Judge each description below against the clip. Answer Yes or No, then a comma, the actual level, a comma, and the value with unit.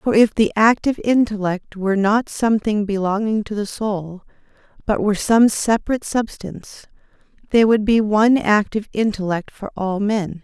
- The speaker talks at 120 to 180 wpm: Yes, average, 150 wpm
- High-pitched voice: Yes, high, 210 Hz